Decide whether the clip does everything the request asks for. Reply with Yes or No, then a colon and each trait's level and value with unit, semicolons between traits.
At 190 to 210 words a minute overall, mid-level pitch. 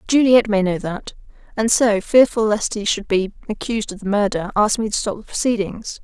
No: average, 200 wpm; high, 210 Hz